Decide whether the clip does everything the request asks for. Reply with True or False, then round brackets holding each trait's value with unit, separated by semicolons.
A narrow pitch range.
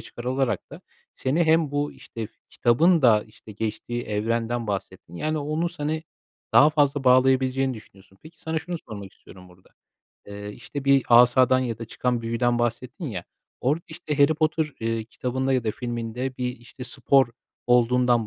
False (3.8 semitones)